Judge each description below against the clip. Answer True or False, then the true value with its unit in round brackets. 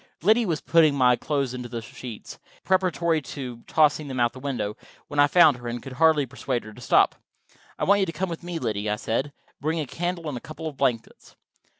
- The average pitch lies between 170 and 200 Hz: False (140 Hz)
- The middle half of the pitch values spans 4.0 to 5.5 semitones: True (5.1 semitones)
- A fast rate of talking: True (225 wpm)